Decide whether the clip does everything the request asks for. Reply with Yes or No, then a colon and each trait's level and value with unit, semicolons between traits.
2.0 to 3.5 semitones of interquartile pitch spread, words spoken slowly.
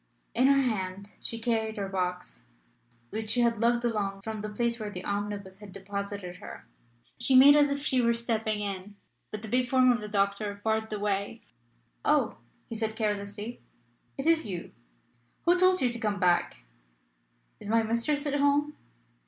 No: average, 3.1 semitones; average, 175 wpm